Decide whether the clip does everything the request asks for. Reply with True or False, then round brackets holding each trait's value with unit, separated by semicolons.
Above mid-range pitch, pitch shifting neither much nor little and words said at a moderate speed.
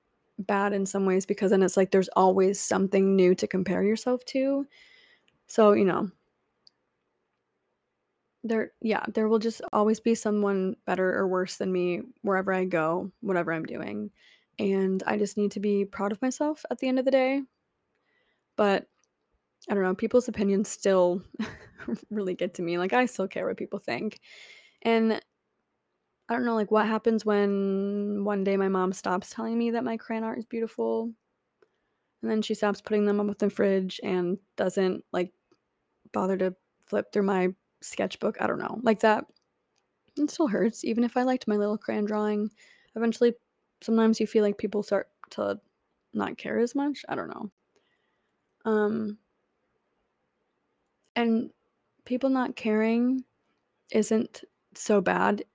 True (210 Hz; 3.0 semitones; 160 wpm)